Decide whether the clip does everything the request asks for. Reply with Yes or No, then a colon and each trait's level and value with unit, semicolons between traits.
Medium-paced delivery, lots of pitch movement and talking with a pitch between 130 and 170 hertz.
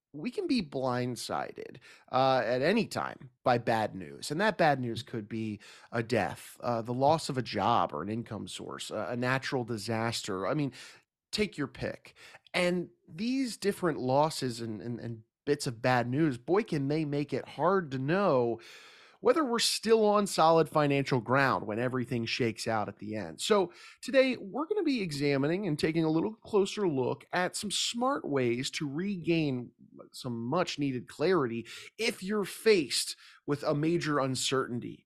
Yes: average, 170 wpm; wide, 7.3 semitones; medium, 140 Hz